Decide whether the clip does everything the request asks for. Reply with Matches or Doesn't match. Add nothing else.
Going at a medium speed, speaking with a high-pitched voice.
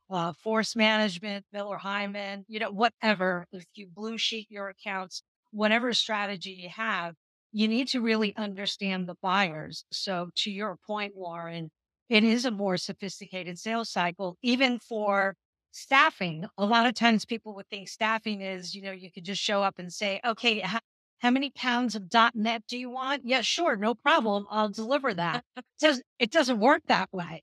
Matches